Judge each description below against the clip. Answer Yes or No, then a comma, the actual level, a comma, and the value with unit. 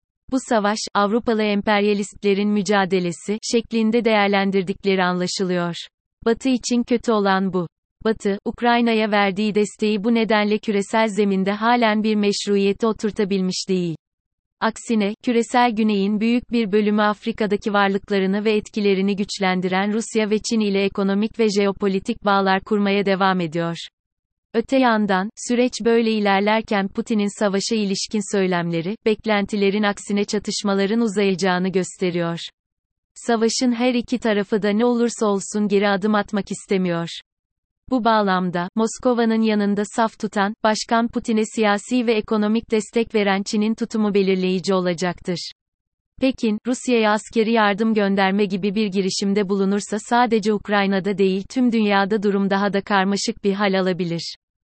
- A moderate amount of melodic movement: No, narrow, 2.2 semitones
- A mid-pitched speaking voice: No, high, 205 Hz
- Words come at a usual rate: Yes, average, 125 wpm